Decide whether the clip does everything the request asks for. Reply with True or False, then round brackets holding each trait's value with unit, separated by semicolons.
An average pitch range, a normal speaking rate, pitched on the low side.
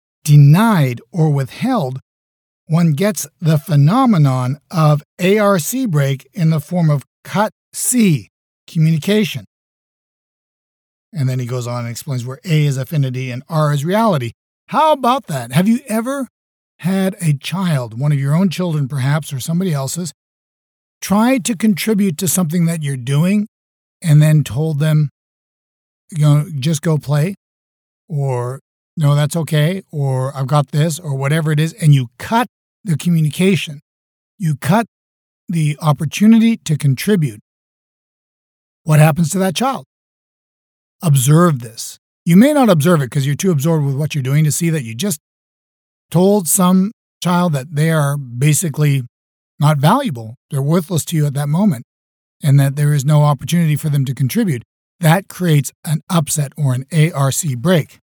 False (4.4 semitones; 155 wpm; 155 Hz)